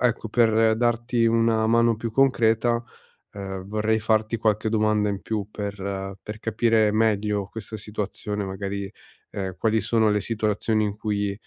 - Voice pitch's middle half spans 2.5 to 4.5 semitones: No, narrow, 1.8 semitones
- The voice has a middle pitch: No, low, 110 Hz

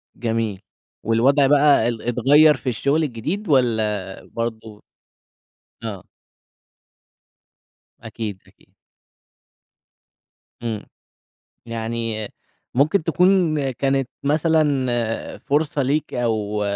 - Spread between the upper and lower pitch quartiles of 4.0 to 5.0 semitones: Yes, average, 4.7 semitones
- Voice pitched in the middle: No, low, 120 Hz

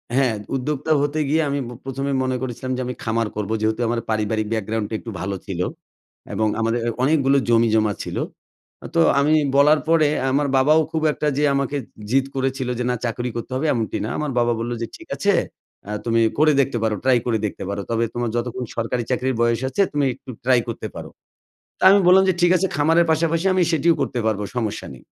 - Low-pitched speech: Yes, low, 130 Hz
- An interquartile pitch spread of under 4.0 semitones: No, average, 4.4 semitones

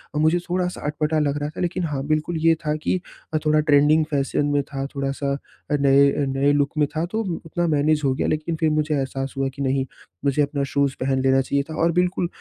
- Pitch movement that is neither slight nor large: No, narrow, 2.2 semitones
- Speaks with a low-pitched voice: No, medium, 145 Hz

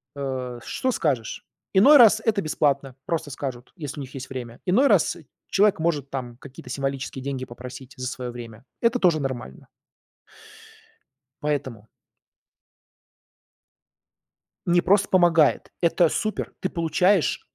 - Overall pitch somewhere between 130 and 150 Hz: Yes, medium, 140 Hz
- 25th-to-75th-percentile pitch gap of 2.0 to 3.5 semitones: No, wide, 5.6 semitones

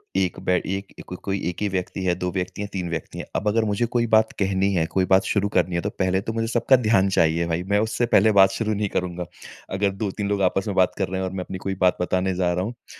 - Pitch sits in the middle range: No, very low, 95 Hz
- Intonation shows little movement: Yes, narrow, 2.1 semitones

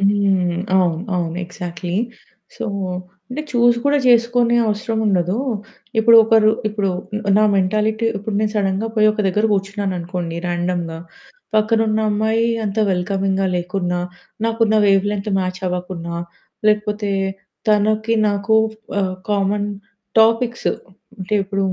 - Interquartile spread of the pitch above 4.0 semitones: No, average, 3.0 semitones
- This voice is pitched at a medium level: No, high, 205 Hz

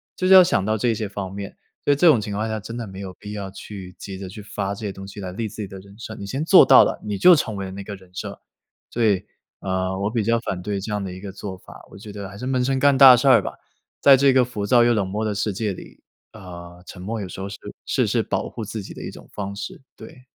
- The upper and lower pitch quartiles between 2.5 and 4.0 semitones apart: Yes, average, 2.9 semitones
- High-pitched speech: No, low, 105 Hz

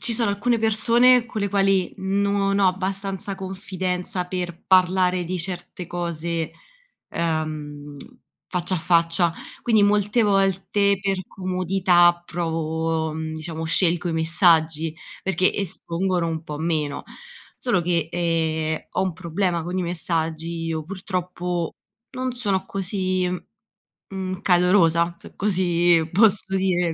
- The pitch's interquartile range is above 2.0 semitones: Yes, average, 2.7 semitones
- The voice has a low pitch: No, medium, 180 Hz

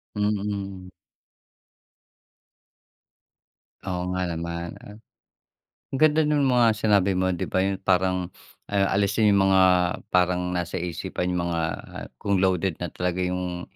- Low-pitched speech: Yes, very low, 95 Hz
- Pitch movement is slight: Yes, narrow, 2.1 semitones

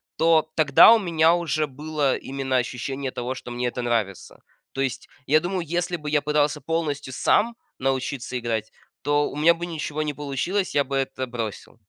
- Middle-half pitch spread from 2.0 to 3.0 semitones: No, average, 3.6 semitones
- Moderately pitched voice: Yes, medium, 145 Hz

